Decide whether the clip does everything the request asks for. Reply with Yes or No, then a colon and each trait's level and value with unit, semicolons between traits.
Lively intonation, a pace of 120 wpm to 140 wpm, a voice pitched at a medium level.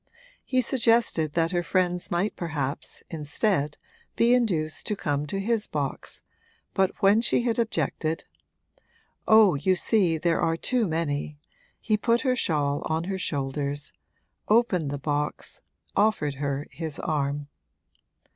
Yes: wide, 6.3 semitones; slow, 135 wpm; medium, 165 Hz